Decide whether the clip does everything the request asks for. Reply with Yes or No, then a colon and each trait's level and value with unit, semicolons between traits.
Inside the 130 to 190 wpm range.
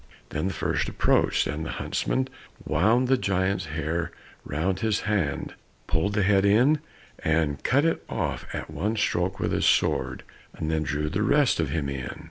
Yes: average, 175 wpm